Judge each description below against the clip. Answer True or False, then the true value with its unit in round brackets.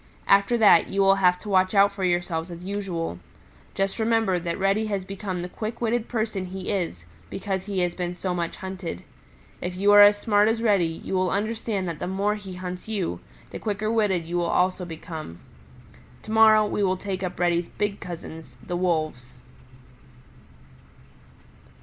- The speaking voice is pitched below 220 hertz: True (190 Hz)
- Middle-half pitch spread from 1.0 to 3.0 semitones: True (2.7 semitones)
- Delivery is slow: False (180 wpm)